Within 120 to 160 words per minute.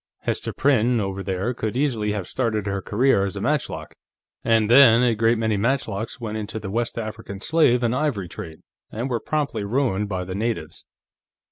No: average, 180 wpm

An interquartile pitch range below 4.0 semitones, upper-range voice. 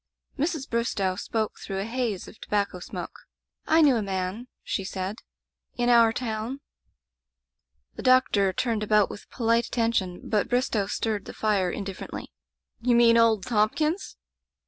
Yes: average, 3.6 semitones; high, 220 Hz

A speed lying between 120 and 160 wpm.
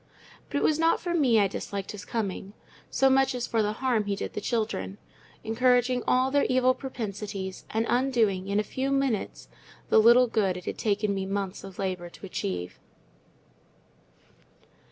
No: average, 170 wpm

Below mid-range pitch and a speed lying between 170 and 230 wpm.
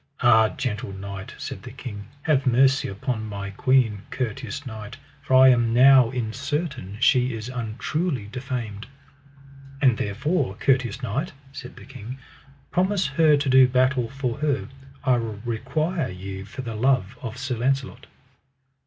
No: low, 125 Hz; average, 145 wpm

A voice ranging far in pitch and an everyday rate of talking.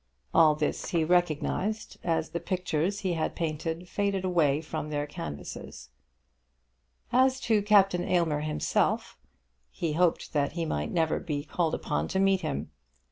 No: average, 3.6 semitones; average, 145 wpm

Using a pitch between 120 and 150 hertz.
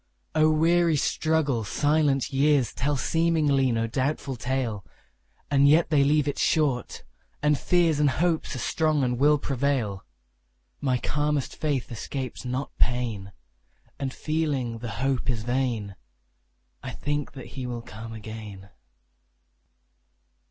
Yes: low, 135 Hz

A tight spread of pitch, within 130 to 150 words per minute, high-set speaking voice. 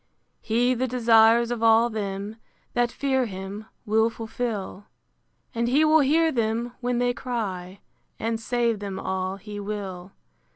No: average, 3.1 semitones; average, 140 wpm; high, 225 Hz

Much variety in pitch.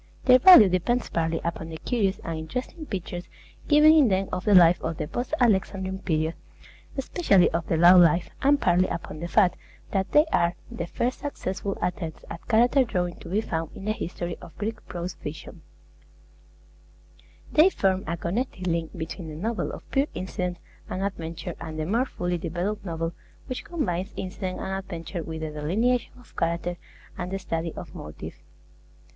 No: average, 4.3 semitones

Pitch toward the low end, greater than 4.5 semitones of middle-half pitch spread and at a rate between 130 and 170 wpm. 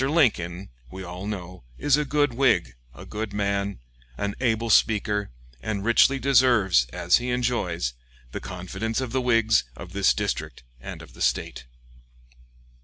Yes: low, 105 Hz; average, 5.0 semitones; average, 150 wpm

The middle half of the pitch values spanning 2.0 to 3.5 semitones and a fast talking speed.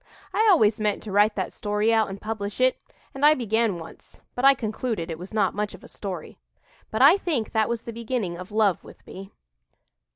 Yes: average, 2.8 semitones; fast, 215 wpm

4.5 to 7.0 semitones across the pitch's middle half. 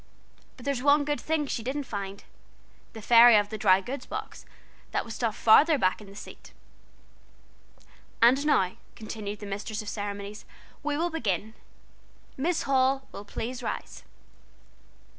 Yes: average, 5.1 semitones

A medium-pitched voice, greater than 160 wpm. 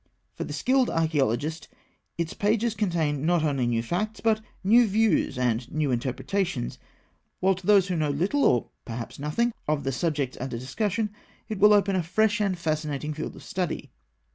Yes: medium, 170 Hz; average, 170 wpm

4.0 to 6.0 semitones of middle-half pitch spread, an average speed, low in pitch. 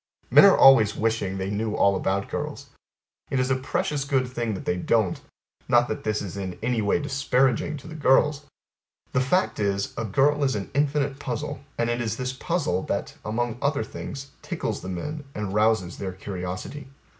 Yes: average, 5.2 semitones; average, 190 wpm; low, 120 Hz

